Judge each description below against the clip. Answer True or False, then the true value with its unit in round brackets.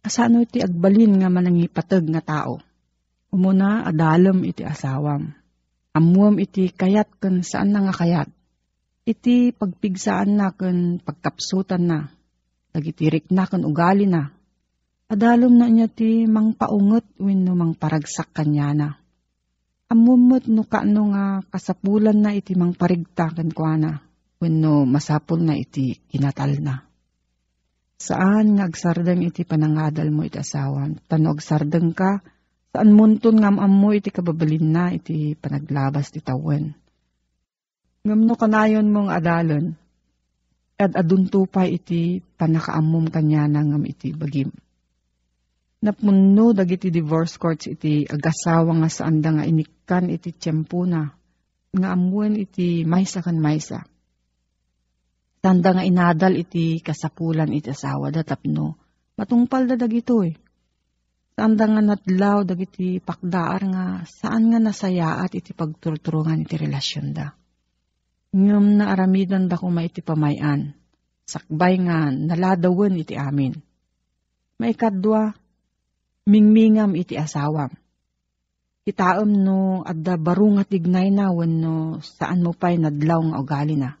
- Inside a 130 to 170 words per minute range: False (120 wpm)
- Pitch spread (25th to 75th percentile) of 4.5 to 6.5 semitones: True (4.9 semitones)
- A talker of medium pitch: True (170 Hz)